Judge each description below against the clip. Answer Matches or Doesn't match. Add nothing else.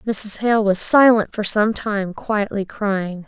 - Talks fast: Doesn't match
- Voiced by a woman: Matches